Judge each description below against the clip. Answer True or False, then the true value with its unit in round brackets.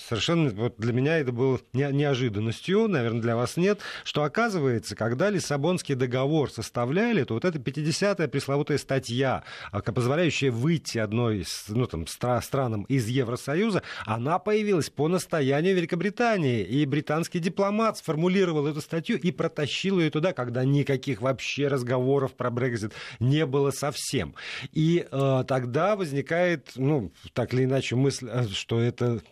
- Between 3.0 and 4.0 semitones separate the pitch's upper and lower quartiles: False (5.0 semitones)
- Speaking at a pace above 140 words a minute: False (135 wpm)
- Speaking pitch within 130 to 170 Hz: True (140 Hz)